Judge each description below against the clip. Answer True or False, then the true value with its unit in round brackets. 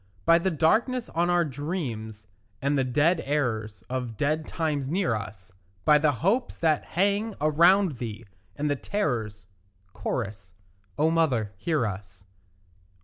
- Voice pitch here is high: False (145 Hz)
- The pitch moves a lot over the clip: True (6.9 semitones)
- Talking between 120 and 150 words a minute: True (140 wpm)